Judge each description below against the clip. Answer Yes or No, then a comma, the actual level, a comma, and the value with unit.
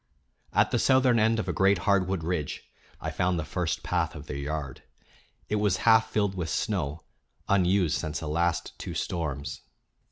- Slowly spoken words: No, average, 170 wpm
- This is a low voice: Yes, very low, 90 Hz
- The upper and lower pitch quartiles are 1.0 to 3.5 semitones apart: No, average, 4.4 semitones